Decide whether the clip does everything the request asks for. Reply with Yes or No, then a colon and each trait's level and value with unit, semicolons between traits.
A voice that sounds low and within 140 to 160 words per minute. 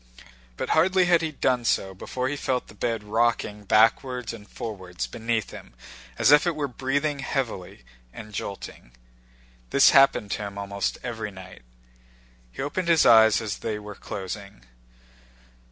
Yes: low, 115 Hz; average, 155 wpm